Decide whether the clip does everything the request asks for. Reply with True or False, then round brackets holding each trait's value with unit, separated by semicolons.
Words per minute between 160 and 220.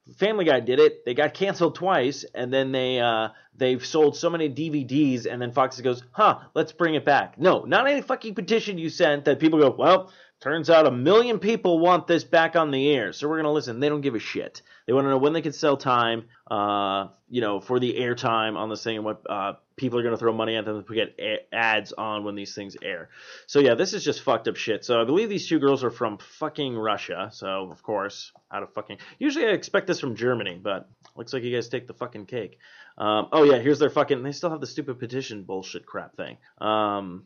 False (240 wpm)